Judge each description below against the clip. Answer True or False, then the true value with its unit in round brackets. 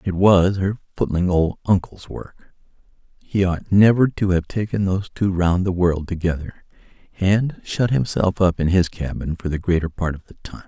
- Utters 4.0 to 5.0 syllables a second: True (4.8 syllables/s)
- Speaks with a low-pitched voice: True (90 Hz)